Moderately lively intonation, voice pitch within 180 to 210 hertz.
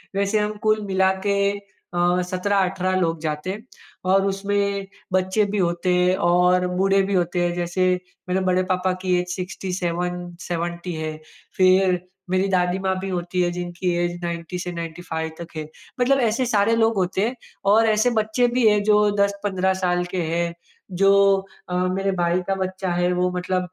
No: narrow, 2.0 semitones; medium, 185 Hz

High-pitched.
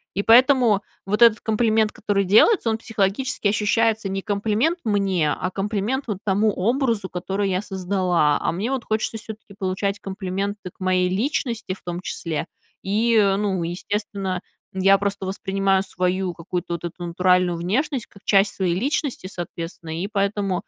Yes: high, 200 Hz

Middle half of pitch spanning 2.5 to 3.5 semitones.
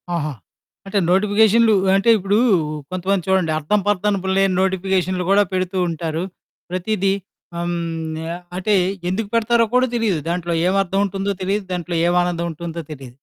Yes: average, 2.8 semitones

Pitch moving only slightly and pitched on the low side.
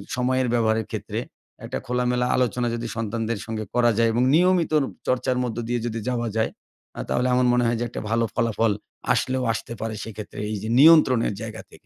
Yes: narrow, 1.9 semitones; low, 120 Hz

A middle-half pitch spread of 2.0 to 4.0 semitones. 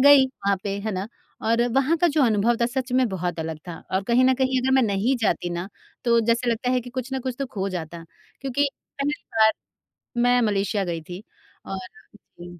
No: average, 5.1 semitones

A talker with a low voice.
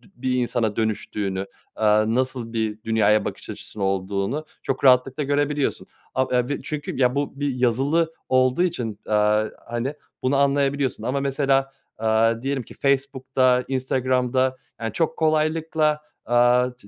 Yes: low, 130 Hz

